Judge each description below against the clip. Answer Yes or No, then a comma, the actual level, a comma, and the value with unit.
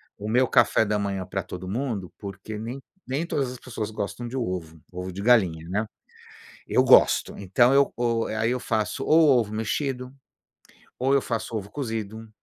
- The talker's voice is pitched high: No, low, 110 Hz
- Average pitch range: Yes, average, 4.1 semitones